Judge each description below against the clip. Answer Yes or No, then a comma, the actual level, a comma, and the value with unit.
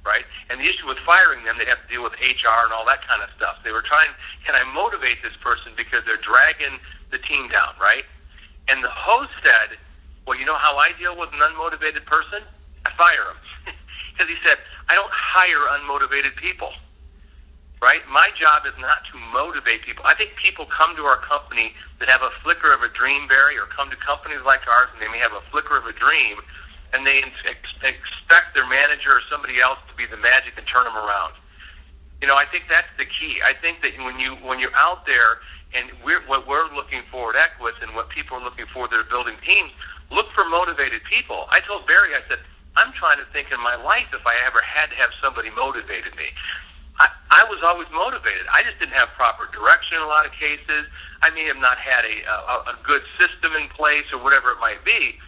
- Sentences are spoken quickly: Yes, fast, 225 wpm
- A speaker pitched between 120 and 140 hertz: Yes, low, 125 Hz